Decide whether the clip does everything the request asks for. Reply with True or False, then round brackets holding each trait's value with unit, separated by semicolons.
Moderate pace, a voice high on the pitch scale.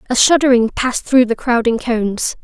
True (175 wpm; 240 Hz)